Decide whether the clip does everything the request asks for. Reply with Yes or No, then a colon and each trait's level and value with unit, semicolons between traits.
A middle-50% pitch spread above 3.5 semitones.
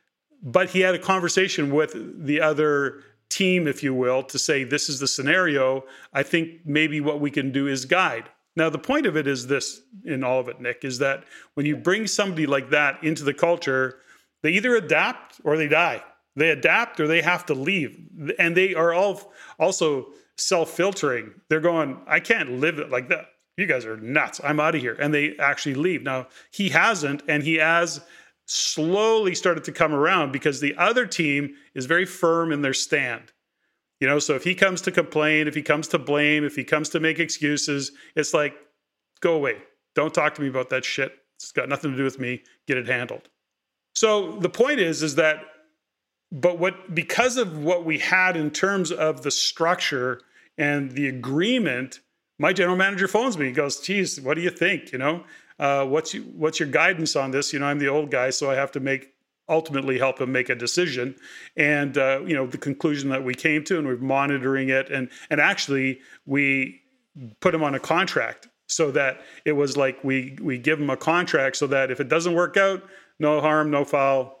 Yes: average, 4.0 semitones